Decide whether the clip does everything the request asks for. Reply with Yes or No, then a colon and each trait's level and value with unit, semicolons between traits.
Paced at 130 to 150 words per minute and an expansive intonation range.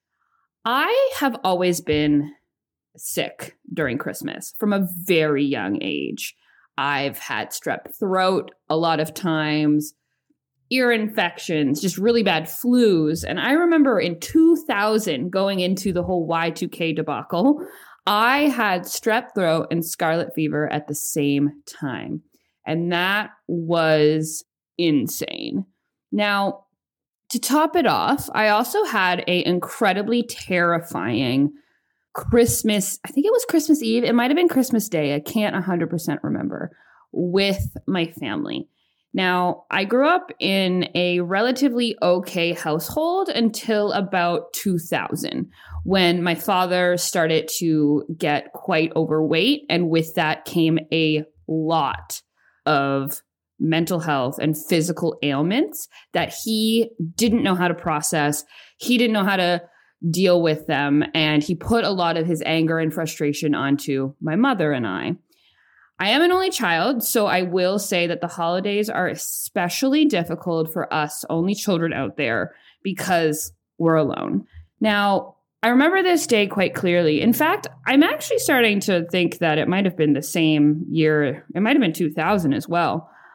Yes: average, 145 wpm; wide, 6.0 semitones